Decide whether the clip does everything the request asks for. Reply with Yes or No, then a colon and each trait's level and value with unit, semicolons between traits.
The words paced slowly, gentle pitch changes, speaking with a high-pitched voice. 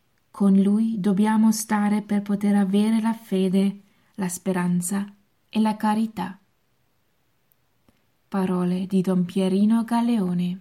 Yes: slow, 100 wpm; narrow, 2.3 semitones; high, 200 Hz